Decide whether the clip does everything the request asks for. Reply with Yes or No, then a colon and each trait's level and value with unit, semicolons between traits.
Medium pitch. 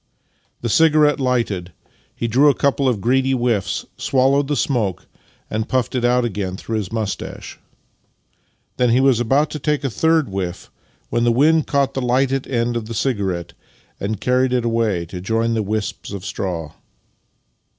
No: low, 120 Hz